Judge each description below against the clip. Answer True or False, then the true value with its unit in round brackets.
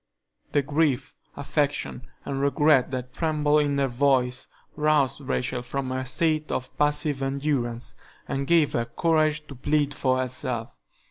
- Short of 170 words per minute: True (140 wpm)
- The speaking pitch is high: False (140 Hz)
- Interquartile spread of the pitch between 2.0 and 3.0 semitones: True (2.6 semitones)